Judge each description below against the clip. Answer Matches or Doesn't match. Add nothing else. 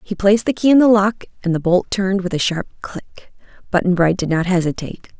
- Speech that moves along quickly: Matches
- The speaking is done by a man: Doesn't match